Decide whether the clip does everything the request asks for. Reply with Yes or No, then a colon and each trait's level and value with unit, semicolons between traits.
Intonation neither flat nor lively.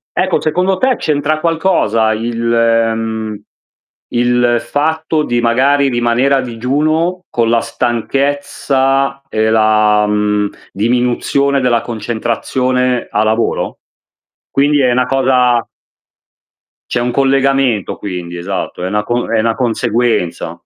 Yes: average, 3.5 semitones